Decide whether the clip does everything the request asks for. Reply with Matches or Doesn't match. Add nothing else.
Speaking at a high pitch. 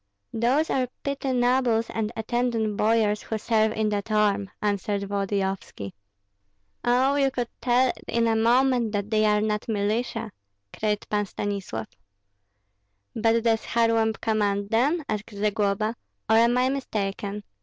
Matches